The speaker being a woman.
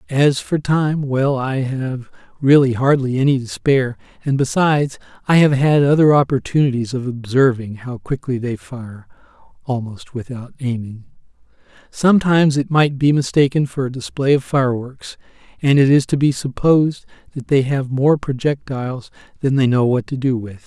No: male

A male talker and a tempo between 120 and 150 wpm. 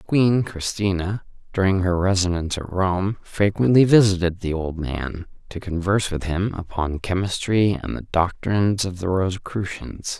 Yes: male; average, 140 wpm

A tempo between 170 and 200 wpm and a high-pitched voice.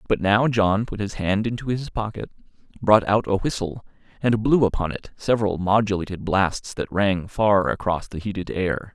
No: average, 180 wpm; low, 105 Hz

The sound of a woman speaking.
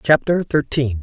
No: male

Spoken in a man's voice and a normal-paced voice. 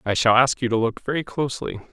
No: male; fast, 250 wpm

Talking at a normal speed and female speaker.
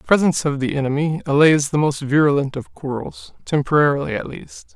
No: average, 175 wpm; male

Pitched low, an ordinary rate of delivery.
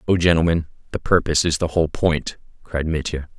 Yes: very low, 80 Hz; average, 175 wpm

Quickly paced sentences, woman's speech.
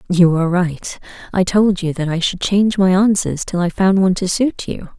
Yes: fast, 230 wpm; female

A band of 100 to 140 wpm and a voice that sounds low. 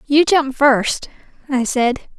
No: slow, 135 wpm; very high, 270 Hz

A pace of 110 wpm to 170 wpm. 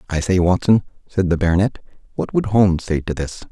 No: fast, 205 wpm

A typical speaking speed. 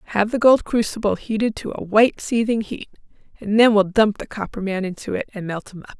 No: fast, 230 wpm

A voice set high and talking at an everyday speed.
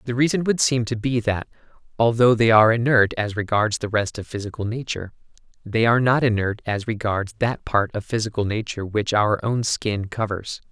No: low, 110 Hz; average, 190 wpm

